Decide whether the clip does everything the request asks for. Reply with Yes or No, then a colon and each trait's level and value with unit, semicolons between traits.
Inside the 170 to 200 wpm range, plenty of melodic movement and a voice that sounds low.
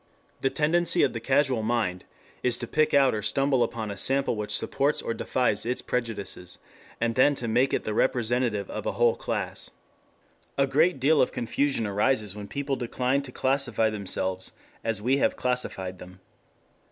No: average, 175 wpm; average, 4.0 semitones; low, 120 Hz